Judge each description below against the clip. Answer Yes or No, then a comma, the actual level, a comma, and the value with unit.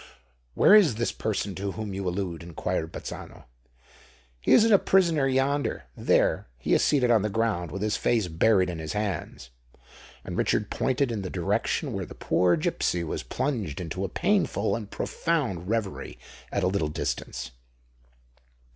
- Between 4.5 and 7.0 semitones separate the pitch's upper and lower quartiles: Yes, wide, 5.4 semitones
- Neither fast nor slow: Yes, average, 160 wpm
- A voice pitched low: Yes, low, 100 Hz